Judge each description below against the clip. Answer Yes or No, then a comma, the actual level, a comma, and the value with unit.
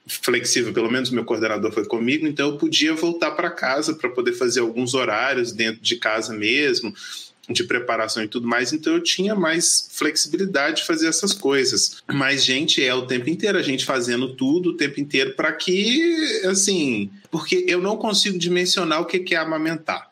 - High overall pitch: No, medium, 160 Hz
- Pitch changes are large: Yes, wide, 8.7 semitones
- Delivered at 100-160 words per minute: No, average, 180 wpm